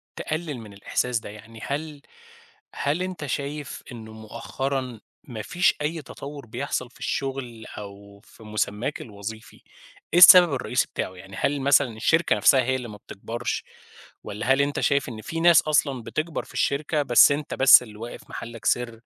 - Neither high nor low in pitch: No, low, 130 Hz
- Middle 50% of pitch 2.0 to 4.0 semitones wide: No, average, 4.6 semitones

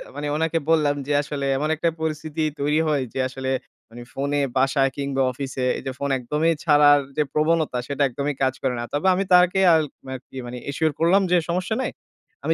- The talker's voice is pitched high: No, medium, 145 Hz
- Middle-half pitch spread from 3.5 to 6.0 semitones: No, average, 2.8 semitones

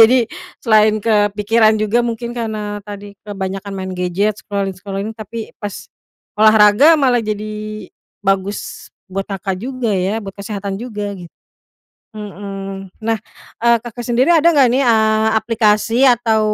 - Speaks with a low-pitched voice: No, high, 215 Hz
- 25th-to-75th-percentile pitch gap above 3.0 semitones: No, narrow, 2.4 semitones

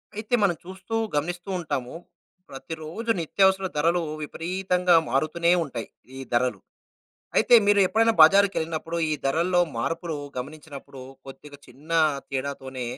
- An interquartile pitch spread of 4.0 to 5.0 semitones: Yes, average, 4.7 semitones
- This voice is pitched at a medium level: Yes, medium, 165 Hz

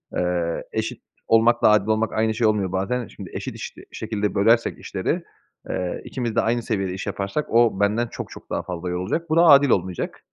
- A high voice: No, low, 105 Hz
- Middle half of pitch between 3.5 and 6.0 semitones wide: Yes, average, 3.8 semitones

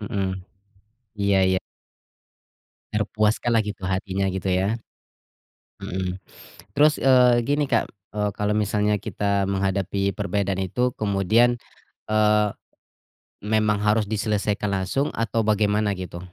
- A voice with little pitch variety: Yes, narrow, 1.9 semitones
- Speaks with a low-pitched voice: Yes, low, 105 Hz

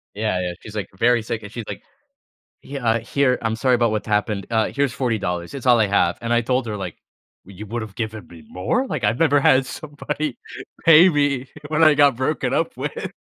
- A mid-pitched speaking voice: No, low, 115 Hz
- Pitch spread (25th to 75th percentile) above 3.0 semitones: Yes, average, 4.6 semitones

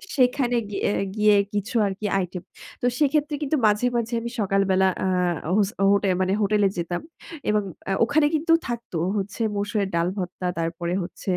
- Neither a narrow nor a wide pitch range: Yes, average, 4.1 semitones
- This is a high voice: Yes, high, 205 Hz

